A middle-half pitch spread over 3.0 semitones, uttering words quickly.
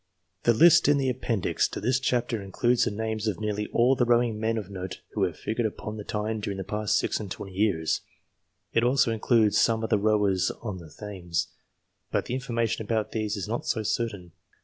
No: narrow, 2.6 semitones; fast, 210 wpm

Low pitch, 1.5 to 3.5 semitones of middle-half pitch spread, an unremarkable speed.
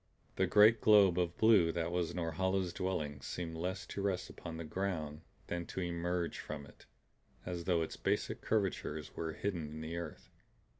Yes: very low, 85 Hz; narrow, 2.5 semitones; average, 170 wpm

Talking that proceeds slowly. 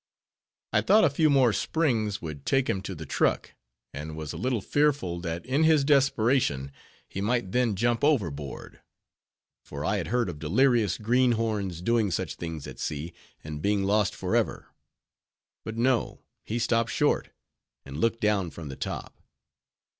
No: average, 160 wpm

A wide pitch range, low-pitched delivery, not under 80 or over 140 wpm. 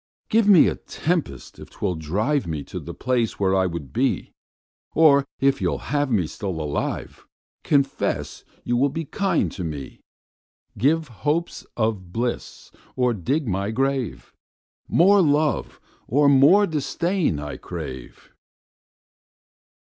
Yes: wide, 8.3 semitones; low, 130 Hz; slow, 135 wpm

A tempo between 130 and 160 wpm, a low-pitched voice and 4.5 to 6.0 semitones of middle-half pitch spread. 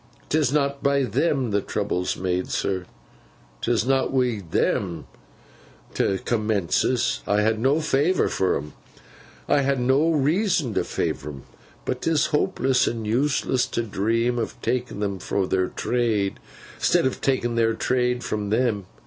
Yes: average, 140 wpm; low, 120 Hz; average, 4.9 semitones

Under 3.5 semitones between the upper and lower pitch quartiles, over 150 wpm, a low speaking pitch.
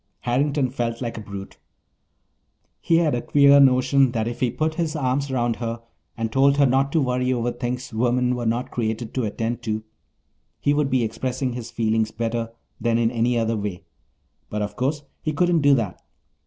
Yes: average, 3.0 semitones; average, 190 wpm; low, 125 Hz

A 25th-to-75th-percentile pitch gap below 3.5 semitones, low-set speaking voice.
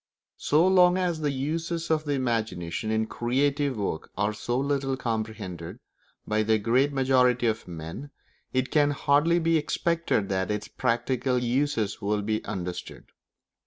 No: average, 5.1 semitones; low, 125 Hz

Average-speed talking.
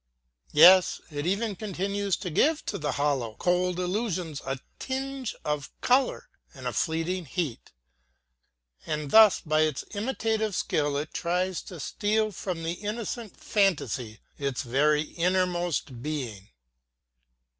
No: slow, 125 wpm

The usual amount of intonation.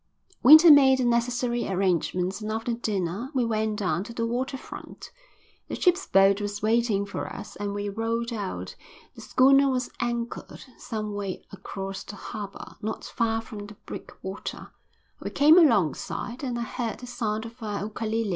Yes: average, 3.0 semitones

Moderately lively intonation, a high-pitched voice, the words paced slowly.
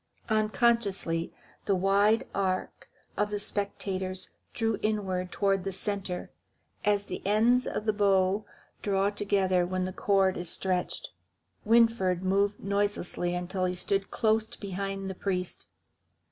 No: narrow, 1.9 semitones; high, 195 Hz; slow, 125 wpm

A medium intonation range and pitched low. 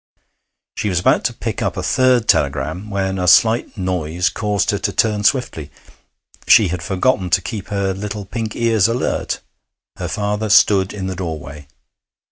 Yes: average, 3.0 semitones; low, 100 Hz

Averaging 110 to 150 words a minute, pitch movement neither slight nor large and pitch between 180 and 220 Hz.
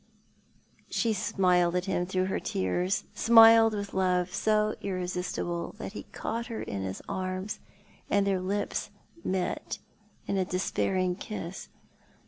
No: slow, 135 wpm; narrow, 2.2 semitones; medium, 185 Hz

